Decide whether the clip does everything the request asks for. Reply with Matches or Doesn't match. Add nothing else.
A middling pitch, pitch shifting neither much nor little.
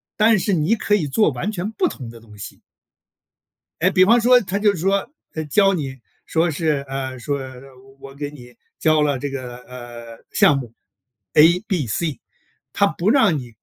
Doesn't match